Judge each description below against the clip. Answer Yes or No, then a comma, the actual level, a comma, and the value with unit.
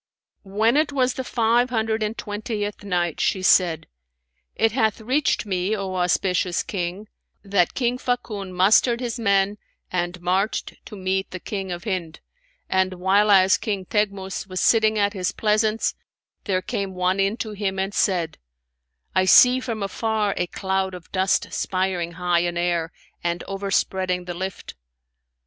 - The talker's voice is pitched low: No, high, 195 Hz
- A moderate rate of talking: Yes, average, 155 wpm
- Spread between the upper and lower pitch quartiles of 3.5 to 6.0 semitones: No, average, 2.9 semitones